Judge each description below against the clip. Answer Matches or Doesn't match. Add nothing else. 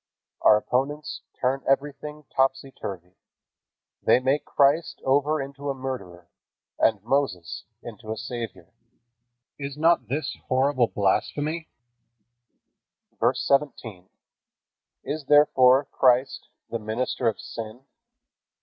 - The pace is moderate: Doesn't match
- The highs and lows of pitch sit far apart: Doesn't match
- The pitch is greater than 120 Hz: Matches